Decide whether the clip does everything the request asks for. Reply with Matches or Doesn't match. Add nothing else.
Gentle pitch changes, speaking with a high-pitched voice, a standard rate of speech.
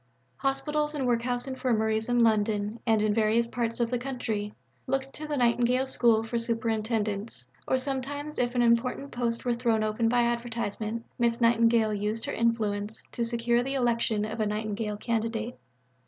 Matches